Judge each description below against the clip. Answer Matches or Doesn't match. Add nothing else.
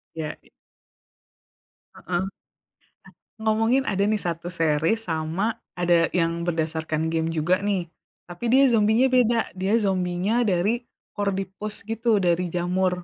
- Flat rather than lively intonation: Doesn't match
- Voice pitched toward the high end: Doesn't match